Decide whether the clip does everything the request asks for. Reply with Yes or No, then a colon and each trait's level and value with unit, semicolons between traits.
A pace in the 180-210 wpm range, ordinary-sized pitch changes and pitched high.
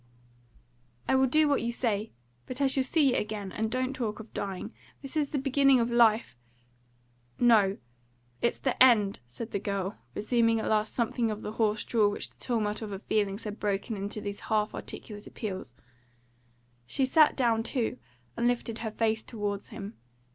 Yes: average, 185 wpm; average, 3.1 semitones; high, 220 Hz